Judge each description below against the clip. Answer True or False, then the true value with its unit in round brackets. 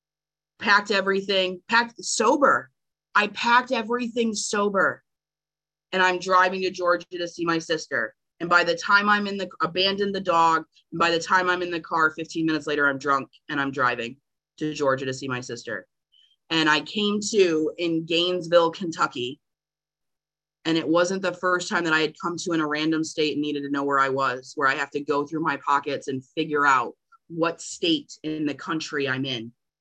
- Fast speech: False (195 wpm)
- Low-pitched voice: False (165 Hz)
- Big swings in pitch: False (3.8 semitones)